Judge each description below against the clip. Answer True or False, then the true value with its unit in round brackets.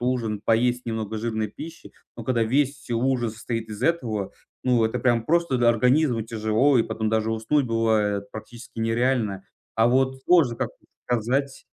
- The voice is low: True (115 Hz)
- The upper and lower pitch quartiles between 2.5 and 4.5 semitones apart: True (2.8 semitones)